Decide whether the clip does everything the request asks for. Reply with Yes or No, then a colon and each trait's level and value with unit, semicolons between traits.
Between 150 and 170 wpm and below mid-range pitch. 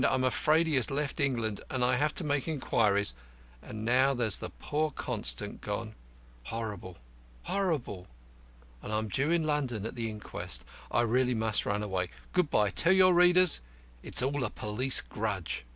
Yes: average, 165 wpm; low, 125 Hz